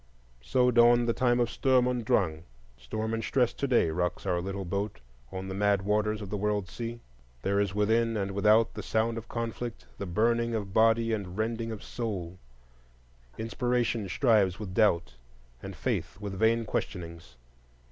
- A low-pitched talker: Yes, low, 105 Hz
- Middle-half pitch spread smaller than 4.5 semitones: Yes, average, 3.3 semitones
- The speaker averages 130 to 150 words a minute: No, average, 170 wpm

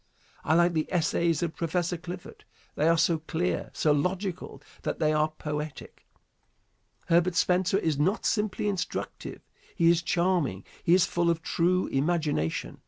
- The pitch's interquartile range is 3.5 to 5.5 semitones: No, narrow, 2.6 semitones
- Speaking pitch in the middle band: Yes, medium, 170 Hz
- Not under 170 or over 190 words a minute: No, average, 150 wpm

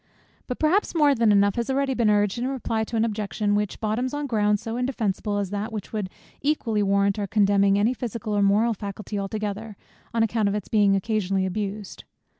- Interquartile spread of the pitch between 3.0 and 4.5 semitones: No, narrow, 2.4 semitones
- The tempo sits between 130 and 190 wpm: No, average, 200 wpm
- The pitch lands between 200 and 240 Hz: Yes, high, 210 Hz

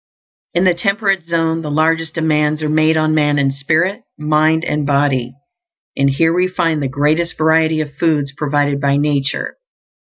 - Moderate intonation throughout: No, narrow, 2.0 semitones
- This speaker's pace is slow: No, average, 165 wpm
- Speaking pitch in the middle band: Yes, medium, 155 Hz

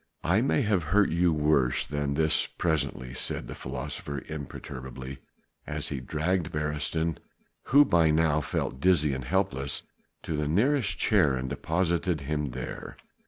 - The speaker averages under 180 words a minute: Yes, average, 150 wpm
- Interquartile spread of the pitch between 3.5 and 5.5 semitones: Yes, average, 3.9 semitones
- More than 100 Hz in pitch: No, very low, 75 Hz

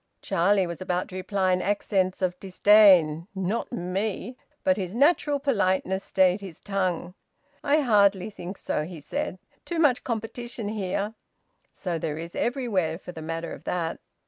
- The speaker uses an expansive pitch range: No, average, 3.4 semitones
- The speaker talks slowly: No, average, 155 wpm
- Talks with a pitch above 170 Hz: Yes, high, 190 Hz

